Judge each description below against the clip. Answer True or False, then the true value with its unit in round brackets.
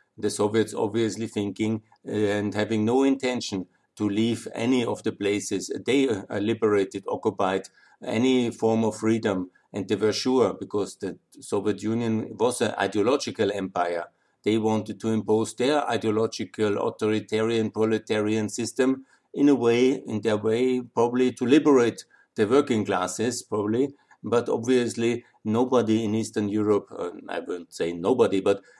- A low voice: True (110 Hz)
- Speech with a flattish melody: True (2.0 semitones)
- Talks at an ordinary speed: True (140 wpm)